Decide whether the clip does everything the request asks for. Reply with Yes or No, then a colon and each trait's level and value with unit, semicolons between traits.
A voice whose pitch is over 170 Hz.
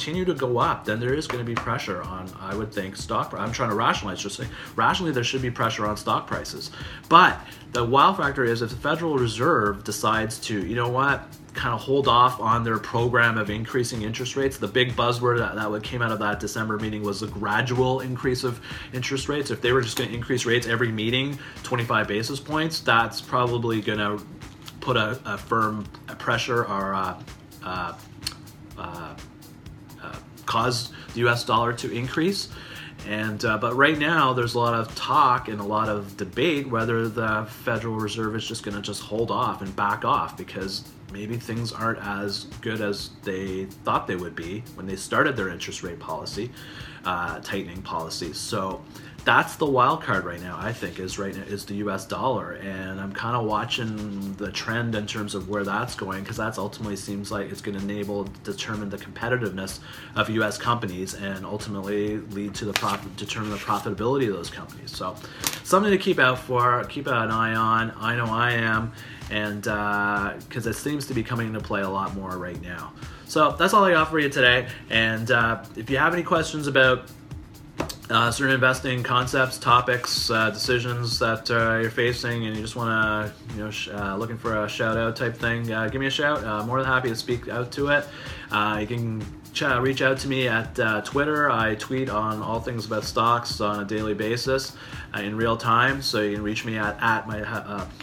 No: low, 115 Hz